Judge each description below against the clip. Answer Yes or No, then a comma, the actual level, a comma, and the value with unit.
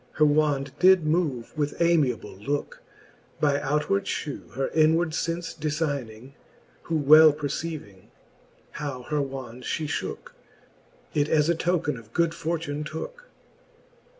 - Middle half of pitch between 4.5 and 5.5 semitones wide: No, average, 2.7 semitones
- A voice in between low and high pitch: Yes, medium, 150 Hz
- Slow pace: Yes, slow, 125 wpm